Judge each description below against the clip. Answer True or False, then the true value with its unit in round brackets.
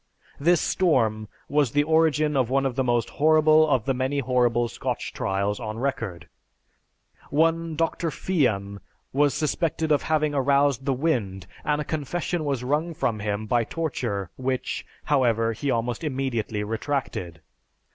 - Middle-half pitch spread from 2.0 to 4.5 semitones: False (4.9 semitones)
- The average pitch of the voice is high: False (135 Hz)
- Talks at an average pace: True (145 wpm)